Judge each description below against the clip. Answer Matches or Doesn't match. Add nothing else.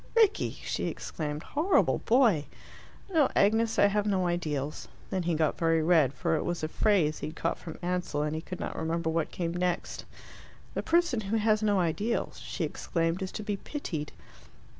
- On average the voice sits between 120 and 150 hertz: Doesn't match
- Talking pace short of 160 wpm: Doesn't match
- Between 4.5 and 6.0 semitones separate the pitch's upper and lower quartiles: Matches